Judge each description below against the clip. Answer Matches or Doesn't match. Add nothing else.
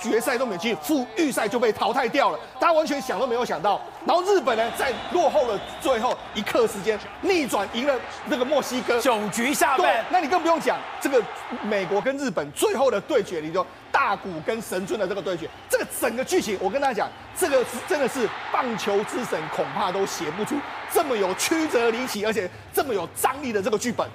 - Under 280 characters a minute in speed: Doesn't match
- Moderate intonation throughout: Doesn't match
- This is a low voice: Doesn't match